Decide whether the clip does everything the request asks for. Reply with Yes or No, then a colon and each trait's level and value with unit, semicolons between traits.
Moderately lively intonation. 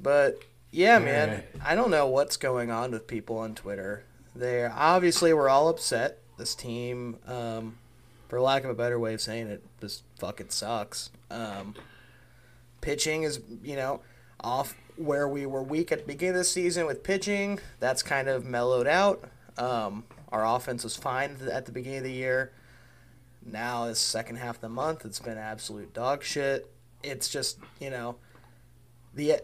Yes: average, 3.3 semitones